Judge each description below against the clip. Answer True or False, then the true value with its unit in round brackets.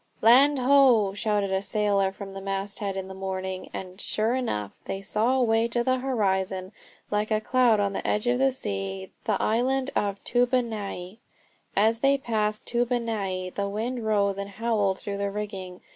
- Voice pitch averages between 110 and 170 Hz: False (210 Hz)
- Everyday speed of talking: True (170 wpm)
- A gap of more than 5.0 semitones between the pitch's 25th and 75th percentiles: False (3.5 semitones)